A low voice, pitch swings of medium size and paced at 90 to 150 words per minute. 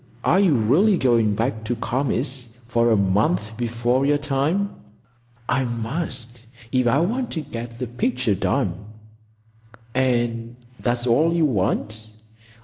Yes: low, 120 Hz; average, 3.3 semitones; slow, 135 wpm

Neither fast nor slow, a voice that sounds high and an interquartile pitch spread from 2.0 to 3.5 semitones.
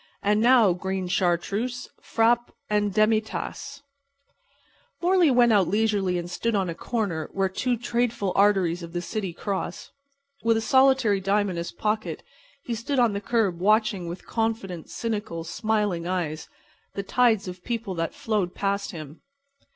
No: average, 160 wpm; high, 205 Hz; average, 4.0 semitones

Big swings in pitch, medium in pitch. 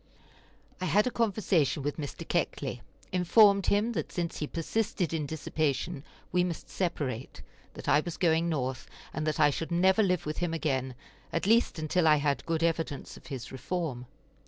No: average, 3.7 semitones; medium, 165 Hz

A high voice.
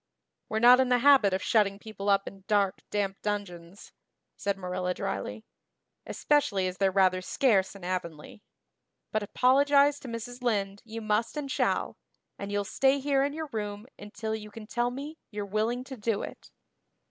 Yes: high, 215 Hz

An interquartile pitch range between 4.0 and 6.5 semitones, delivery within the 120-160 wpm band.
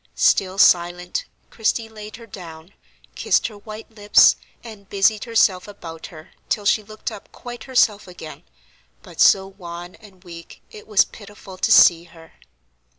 No: average, 3.4 semitones; average, 150 wpm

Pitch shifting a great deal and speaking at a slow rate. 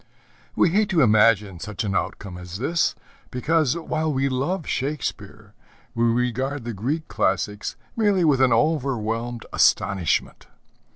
Yes: wide, 6.3 semitones; slow, 130 wpm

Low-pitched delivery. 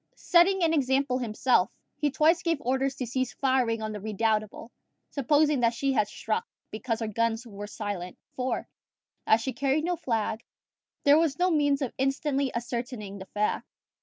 No: very high, 255 Hz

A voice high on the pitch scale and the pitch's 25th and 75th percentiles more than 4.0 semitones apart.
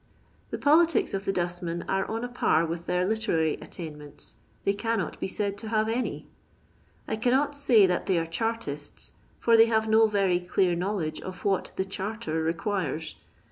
Yes: high, 195 Hz; average, 4.5 semitones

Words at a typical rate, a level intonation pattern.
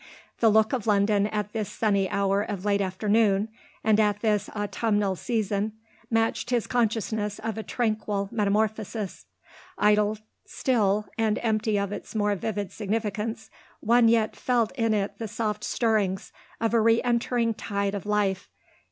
Yes: average, 150 wpm; narrow, 1.8 semitones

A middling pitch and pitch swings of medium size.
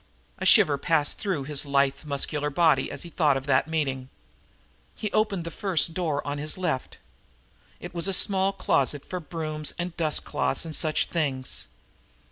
Yes: medium, 155 Hz; average, 3.4 semitones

